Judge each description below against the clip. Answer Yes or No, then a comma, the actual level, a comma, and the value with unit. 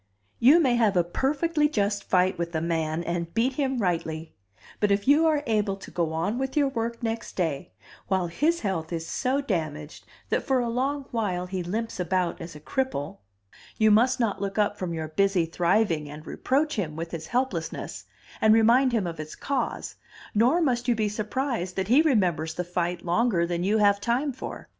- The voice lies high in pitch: Yes, high, 205 Hz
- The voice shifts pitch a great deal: Yes, wide, 6.6 semitones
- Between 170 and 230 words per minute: Yes, average, 195 wpm